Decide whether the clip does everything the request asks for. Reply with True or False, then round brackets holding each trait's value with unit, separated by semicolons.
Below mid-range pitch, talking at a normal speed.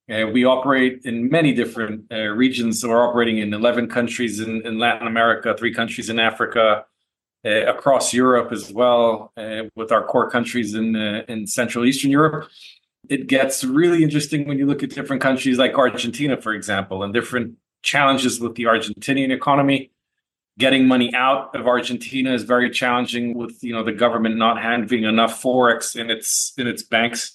True (120 Hz; 180 wpm)